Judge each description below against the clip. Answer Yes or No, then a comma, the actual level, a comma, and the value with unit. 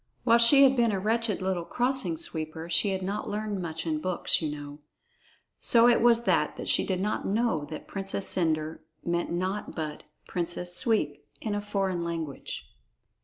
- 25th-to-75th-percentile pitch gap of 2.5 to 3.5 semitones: No, average, 5.1 semitones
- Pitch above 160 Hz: Yes, high, 190 Hz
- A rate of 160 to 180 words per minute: Yes, average, 170 wpm